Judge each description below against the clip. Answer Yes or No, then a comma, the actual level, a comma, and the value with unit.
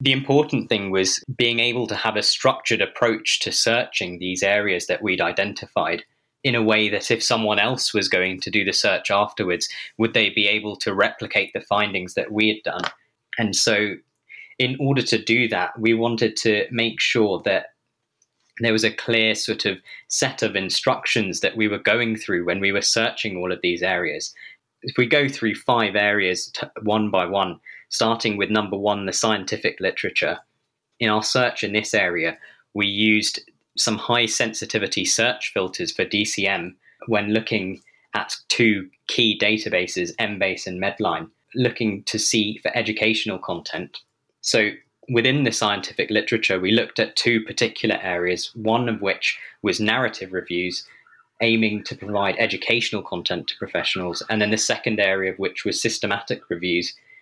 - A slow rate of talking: No, average, 170 wpm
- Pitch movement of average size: No, narrow, 2.3 semitones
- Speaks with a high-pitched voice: No, low, 110 Hz